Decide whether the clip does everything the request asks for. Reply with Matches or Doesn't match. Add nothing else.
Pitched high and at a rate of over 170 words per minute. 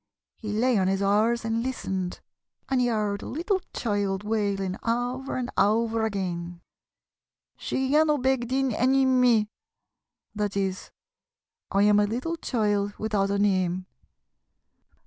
Doesn't match